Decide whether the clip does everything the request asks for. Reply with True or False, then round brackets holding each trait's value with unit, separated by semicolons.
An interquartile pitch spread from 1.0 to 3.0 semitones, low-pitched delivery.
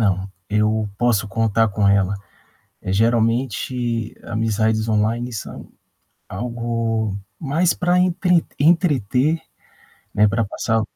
True (2.7 semitones; 115 Hz)